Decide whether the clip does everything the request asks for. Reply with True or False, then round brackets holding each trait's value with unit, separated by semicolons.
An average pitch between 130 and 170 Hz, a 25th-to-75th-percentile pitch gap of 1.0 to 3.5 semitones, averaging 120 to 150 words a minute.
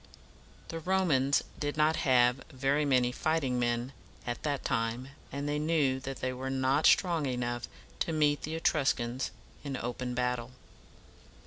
True (135 Hz; 3.2 semitones; 145 wpm)